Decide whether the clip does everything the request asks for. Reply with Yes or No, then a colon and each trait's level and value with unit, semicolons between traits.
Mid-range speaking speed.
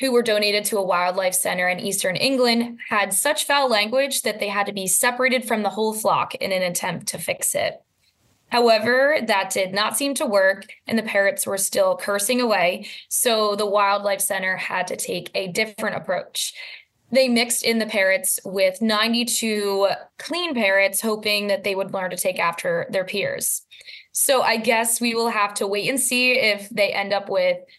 Yes: average, 190 wpm